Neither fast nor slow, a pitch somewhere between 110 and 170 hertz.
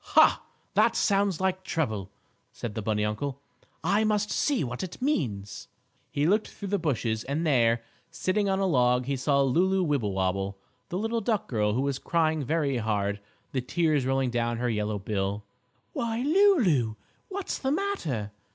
Yes: average, 165 wpm; medium, 140 Hz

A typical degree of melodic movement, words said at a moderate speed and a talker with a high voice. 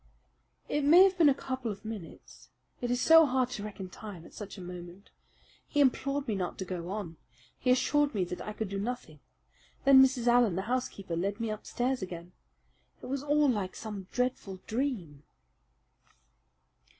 No: wide, 5.7 semitones; average, 175 wpm; high, 220 Hz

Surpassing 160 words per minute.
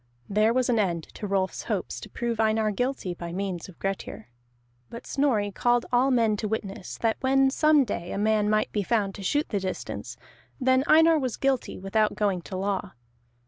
Yes: average, 195 wpm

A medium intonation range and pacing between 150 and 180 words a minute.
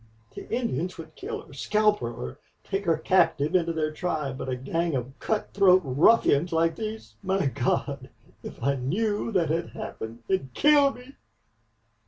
No: wide, 6.4 semitones; average, 165 wpm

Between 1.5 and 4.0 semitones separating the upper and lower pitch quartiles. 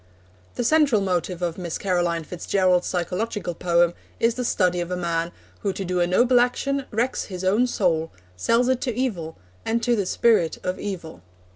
No: average, 5.1 semitones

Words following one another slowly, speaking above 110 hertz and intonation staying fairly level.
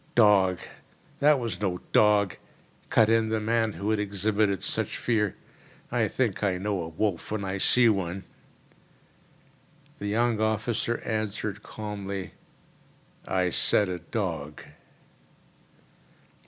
No: slow, 120 wpm; low, 105 Hz; narrow, 2.3 semitones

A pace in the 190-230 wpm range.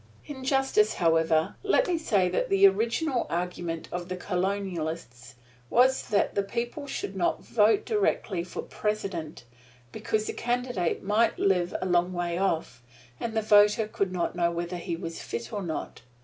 No: average, 165 wpm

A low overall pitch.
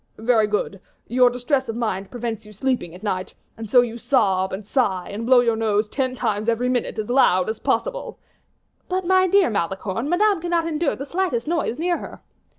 No: high, 240 Hz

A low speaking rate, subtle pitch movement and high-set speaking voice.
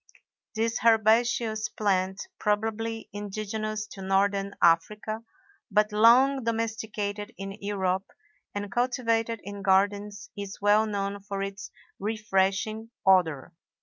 Yes: slow, 105 wpm; narrow, 2.0 semitones; high, 210 Hz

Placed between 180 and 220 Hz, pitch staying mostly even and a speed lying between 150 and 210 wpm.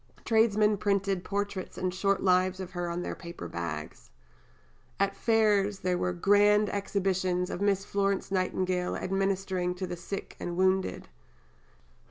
No: high, 190 Hz; narrow, 1.8 semitones; average, 140 wpm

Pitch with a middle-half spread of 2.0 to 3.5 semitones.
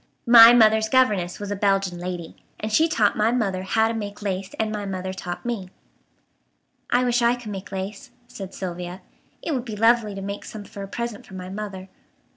Yes: average, 3.2 semitones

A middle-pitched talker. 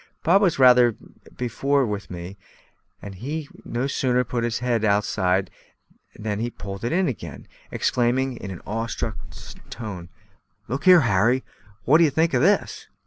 No: low, 120 Hz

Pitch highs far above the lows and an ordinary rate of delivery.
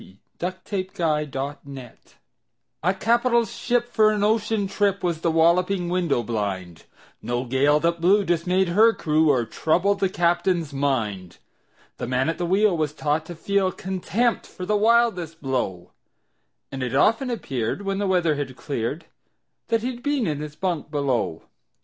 Yes: wide, 5.9 semitones; average, 160 wpm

